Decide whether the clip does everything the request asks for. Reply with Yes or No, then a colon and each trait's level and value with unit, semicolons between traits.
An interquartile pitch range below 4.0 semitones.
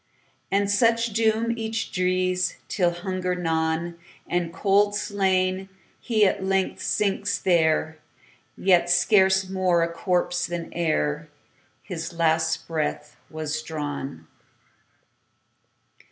Yes: average, 3.0 semitones